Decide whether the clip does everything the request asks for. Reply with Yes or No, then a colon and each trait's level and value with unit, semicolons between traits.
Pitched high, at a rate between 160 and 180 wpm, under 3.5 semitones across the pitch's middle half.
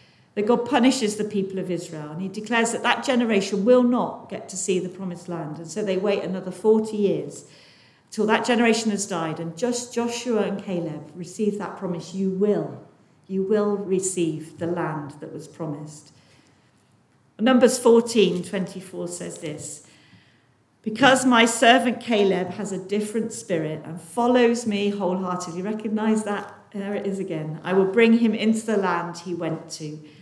No: high, 195 Hz; average, 165 wpm; average, 4.3 semitones